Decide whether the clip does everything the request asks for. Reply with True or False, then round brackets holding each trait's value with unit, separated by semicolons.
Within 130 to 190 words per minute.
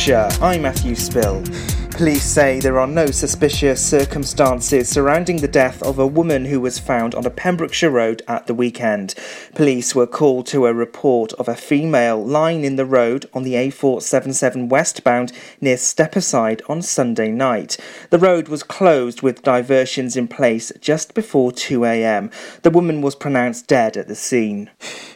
True (160 wpm)